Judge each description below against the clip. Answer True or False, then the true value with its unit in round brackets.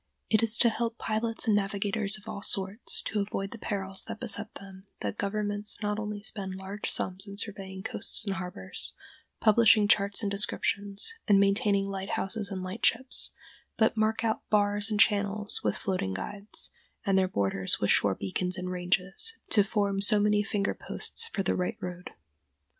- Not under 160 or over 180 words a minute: True (170 wpm)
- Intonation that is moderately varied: False (1.9 semitones)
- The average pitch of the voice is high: True (200 Hz)